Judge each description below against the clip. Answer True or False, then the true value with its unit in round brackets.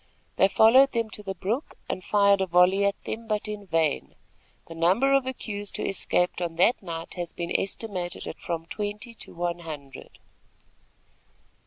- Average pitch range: True (3.7 semitones)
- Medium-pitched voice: False (195 Hz)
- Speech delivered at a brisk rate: False (170 wpm)